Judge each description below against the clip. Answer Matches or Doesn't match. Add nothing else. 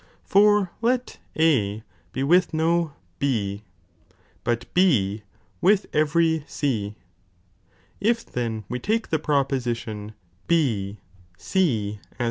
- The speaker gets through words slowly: Matches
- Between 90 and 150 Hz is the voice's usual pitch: Matches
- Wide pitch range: Matches